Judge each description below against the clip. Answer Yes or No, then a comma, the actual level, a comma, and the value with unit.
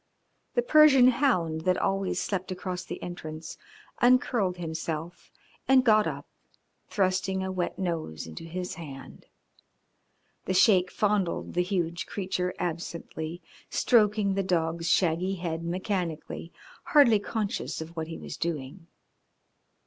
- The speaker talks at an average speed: No, slow, 125 wpm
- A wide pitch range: No, average, 3.3 semitones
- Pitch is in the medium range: Yes, medium, 180 Hz